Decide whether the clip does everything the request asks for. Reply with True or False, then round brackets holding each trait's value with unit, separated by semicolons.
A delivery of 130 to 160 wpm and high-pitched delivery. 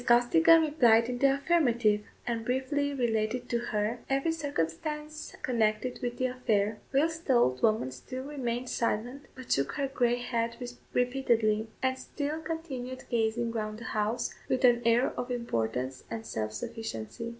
True (150 wpm; 245 Hz)